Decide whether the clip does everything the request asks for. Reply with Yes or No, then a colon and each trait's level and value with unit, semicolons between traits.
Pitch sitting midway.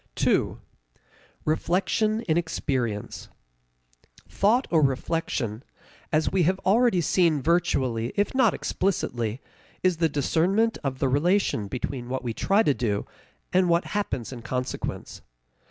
Yes: medium, 160 Hz